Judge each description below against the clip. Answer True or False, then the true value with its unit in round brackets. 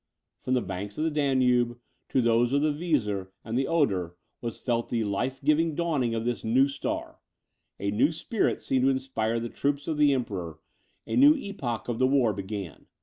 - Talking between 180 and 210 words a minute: True (195 wpm)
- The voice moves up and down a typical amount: True (4.4 semitones)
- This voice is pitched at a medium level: False (125 Hz)